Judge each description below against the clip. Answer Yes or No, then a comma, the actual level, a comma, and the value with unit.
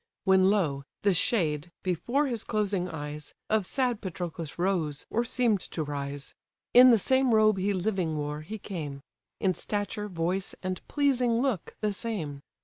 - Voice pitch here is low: No, high, 190 Hz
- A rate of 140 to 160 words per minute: Yes, average, 155 wpm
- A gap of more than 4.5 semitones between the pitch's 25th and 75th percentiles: Yes, wide, 5.4 semitones